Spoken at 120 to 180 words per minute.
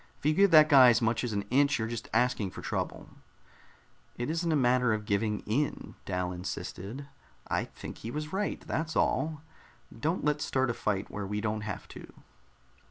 No: average, 190 wpm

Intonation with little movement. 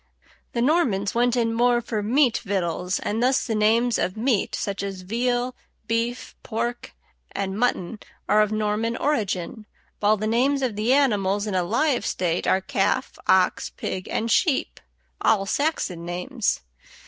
No: average, 3.6 semitones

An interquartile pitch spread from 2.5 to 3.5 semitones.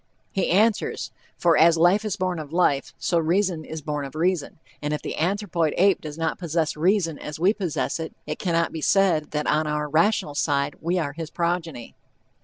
Yes: average, 3.2 semitones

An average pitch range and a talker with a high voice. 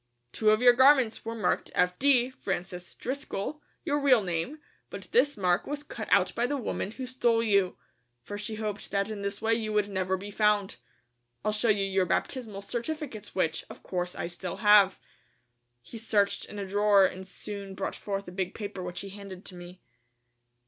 Yes: average, 3.4 semitones; high, 205 Hz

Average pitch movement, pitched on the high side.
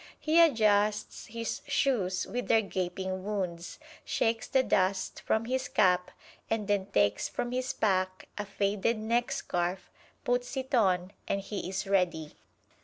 Yes: average, 3.8 semitones; high, 205 Hz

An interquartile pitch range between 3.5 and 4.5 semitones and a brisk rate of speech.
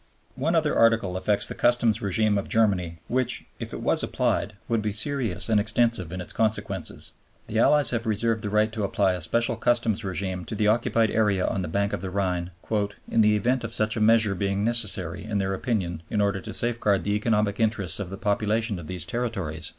No: average, 2.8 semitones; fast, 210 wpm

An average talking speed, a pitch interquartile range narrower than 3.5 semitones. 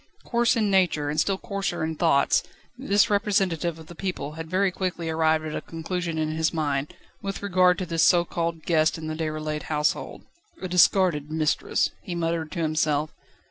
Yes: average, 180 wpm; average, 2.8 semitones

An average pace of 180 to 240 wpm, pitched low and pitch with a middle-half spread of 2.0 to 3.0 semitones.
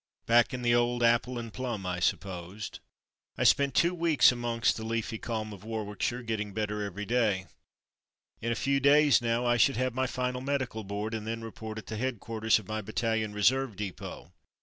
Yes: average, 195 wpm; low, 115 Hz; average, 2.7 semitones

